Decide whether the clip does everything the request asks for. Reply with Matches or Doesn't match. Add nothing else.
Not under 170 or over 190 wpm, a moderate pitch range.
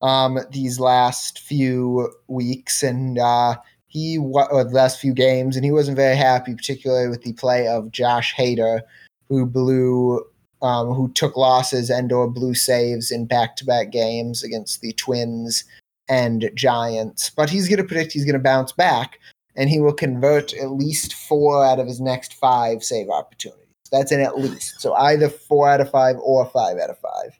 Doesn't match